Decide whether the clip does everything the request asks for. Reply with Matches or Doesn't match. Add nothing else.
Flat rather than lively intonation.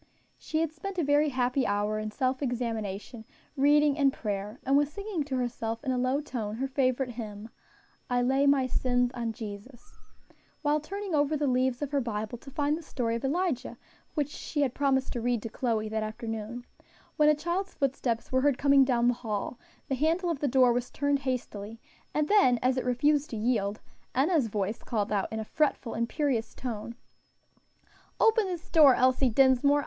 Doesn't match